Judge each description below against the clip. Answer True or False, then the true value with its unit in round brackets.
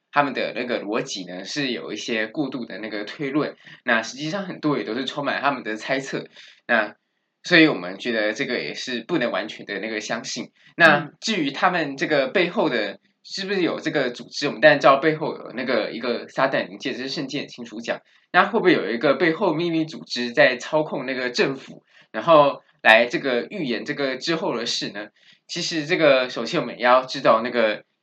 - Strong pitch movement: False (4.2 semitones)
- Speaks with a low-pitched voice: False (145 Hz)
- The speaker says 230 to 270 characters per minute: False (310 characters per minute)